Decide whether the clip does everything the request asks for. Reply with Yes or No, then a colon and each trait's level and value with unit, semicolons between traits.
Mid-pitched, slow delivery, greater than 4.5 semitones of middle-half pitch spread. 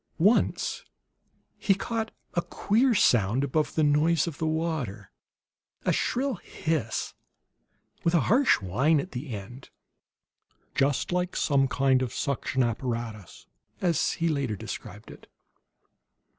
Yes: medium, 145 Hz; slow, 125 wpm; wide, 5.5 semitones